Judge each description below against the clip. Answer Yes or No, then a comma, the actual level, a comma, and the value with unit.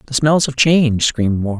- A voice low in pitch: Yes, low, 130 Hz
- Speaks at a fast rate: Yes, fast, 225 wpm